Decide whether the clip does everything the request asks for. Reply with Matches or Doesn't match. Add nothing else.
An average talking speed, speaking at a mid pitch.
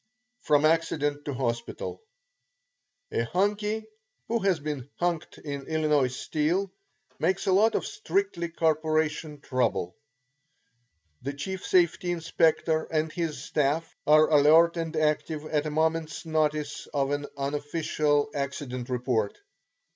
Doesn't match